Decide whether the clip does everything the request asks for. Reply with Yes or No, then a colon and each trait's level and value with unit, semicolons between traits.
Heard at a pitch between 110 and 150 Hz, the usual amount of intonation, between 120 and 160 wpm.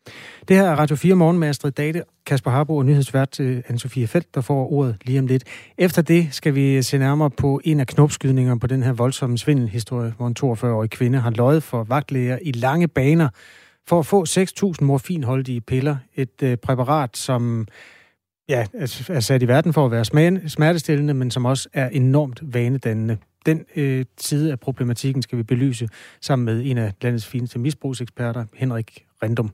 No: low, 135 Hz; average, 3.4 semitones; average, 180 wpm